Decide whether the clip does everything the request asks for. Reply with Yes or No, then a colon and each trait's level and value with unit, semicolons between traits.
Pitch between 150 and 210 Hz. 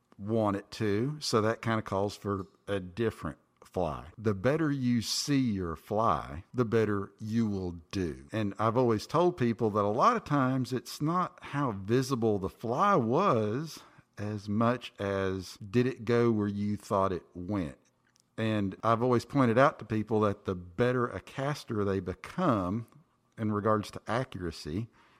No: low, 110 Hz